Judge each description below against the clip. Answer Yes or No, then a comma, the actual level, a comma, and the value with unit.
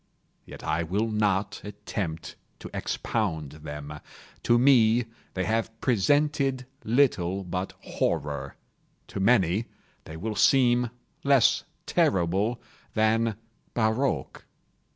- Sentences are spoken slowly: Yes, slow, 95 wpm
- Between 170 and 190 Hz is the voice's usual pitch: No, low, 105 Hz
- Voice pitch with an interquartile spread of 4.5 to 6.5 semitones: Yes, wide, 5.4 semitones